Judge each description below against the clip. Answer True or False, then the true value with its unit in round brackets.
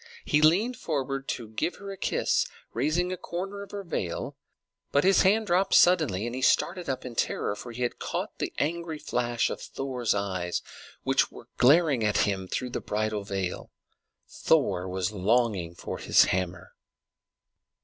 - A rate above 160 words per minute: True (170 wpm)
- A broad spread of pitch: True (8.9 semitones)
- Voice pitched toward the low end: True (125 Hz)